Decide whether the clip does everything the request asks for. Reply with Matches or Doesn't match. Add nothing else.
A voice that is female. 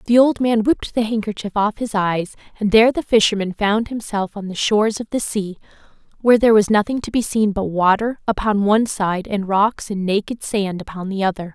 Matches